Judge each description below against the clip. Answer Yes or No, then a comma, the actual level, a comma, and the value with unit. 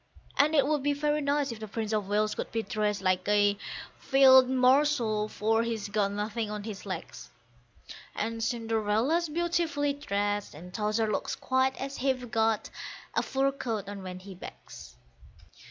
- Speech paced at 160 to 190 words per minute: Yes, average, 170 wpm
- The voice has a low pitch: No, high, 225 Hz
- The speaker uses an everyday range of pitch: Yes, average, 4.6 semitones